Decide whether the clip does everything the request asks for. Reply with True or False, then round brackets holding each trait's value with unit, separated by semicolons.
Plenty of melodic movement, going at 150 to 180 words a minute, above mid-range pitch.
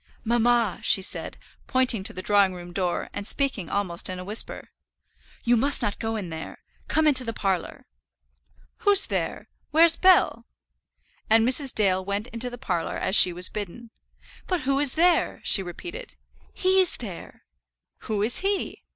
True (6.3 semitones; 160 wpm; 225 Hz)